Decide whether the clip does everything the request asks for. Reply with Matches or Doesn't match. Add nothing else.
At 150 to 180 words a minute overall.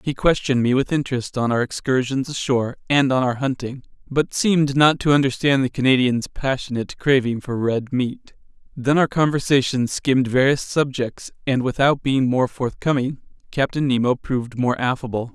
Matches